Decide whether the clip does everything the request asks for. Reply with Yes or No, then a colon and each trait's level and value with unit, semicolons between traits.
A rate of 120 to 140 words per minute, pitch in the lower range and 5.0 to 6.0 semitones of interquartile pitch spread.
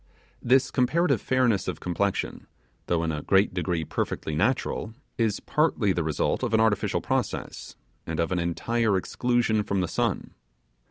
No: average, 155 wpm; low, 100 Hz; wide, 5.5 semitones